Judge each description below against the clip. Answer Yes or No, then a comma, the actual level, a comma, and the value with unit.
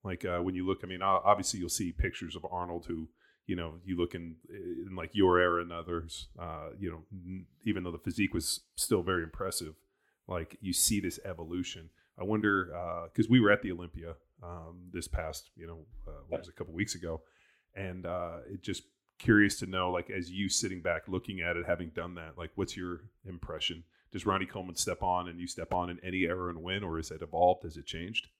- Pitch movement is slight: Yes, narrow, 1.8 semitones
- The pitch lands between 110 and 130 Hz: No, very low, 90 Hz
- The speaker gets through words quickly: Yes, fast, 225 wpm